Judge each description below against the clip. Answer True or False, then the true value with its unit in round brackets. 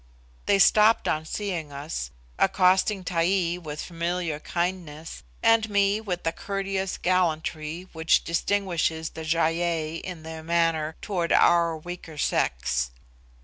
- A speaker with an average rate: False (125 wpm)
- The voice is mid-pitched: True (170 Hz)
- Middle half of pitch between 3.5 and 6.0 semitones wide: False (2.7 semitones)